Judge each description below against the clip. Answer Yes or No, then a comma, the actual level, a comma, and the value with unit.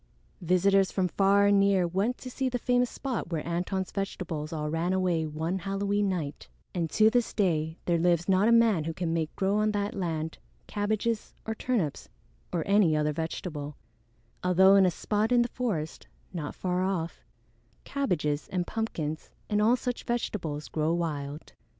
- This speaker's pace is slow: No, average, 170 wpm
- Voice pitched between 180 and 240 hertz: Yes, medium, 185 Hz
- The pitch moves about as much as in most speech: Yes, average, 4.3 semitones